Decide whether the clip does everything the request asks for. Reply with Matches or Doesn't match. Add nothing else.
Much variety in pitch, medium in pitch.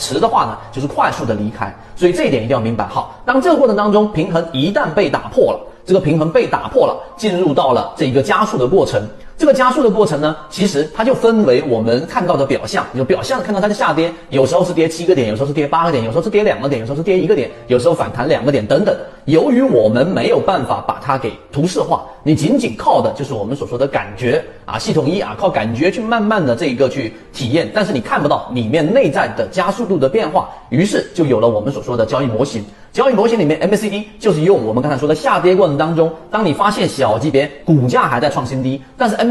Matches